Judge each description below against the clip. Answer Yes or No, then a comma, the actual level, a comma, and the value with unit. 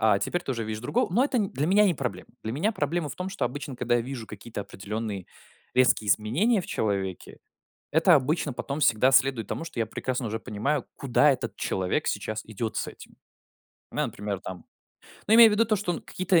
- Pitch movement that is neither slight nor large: No, wide, 7.7 semitones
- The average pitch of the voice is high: No, low, 130 Hz